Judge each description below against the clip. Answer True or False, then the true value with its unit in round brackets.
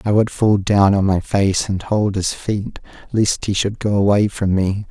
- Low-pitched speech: True (100 Hz)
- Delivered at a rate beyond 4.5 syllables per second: False (4.3 syllables/s)